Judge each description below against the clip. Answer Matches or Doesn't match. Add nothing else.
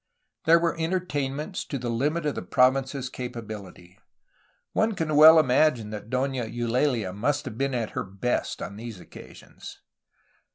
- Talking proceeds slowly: Doesn't match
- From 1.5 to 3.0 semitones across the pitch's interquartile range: Doesn't match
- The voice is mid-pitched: Doesn't match